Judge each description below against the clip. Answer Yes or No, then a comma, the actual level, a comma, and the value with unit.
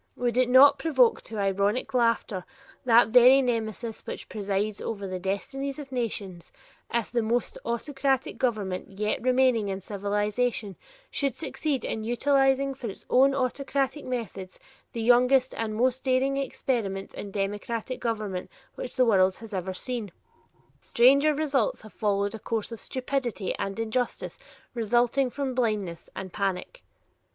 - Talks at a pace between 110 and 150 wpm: Yes, average, 145 wpm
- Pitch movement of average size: Yes, average, 4.2 semitones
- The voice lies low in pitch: No, high, 235 Hz